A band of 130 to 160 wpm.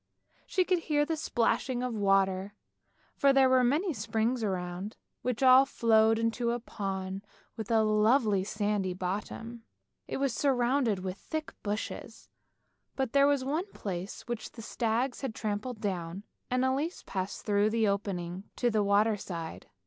Yes: average, 155 wpm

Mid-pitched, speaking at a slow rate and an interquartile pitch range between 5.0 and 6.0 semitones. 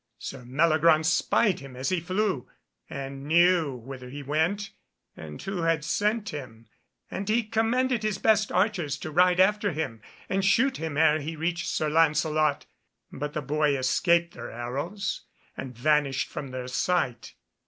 No: medium, 160 Hz; average, 155 wpm; wide, 5.5 semitones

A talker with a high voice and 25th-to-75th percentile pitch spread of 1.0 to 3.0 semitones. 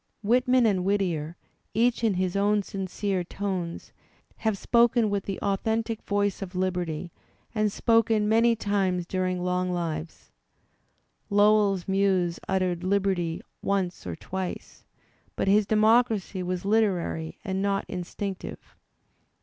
Yes: high, 195 Hz; average, 2.7 semitones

